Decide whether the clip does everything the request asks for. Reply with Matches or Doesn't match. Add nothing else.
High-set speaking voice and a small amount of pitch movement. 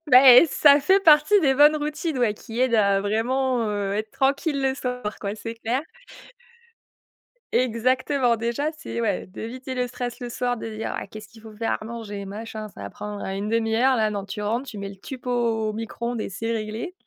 Doesn't match